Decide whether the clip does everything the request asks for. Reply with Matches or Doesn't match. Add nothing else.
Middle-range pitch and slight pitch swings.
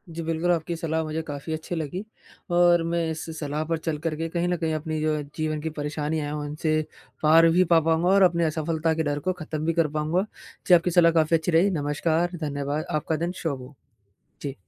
Matches